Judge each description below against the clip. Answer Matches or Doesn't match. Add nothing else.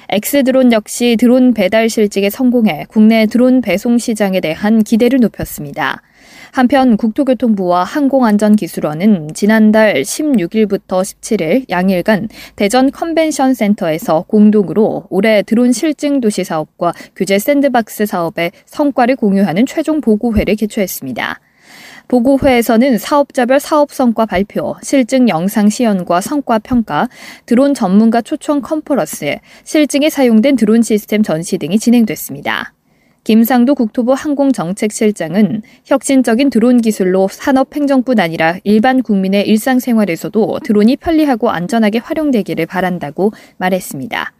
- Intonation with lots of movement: Doesn't match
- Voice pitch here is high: Matches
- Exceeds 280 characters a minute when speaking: Matches